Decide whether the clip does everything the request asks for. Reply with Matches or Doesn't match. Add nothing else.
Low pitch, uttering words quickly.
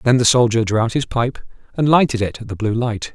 Matches